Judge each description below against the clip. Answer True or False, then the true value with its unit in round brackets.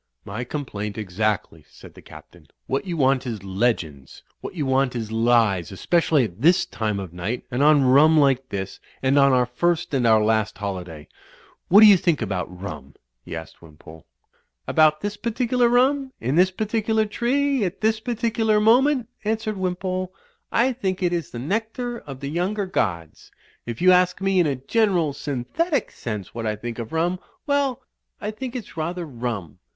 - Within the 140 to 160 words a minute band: False (180 wpm)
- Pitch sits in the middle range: True (150 Hz)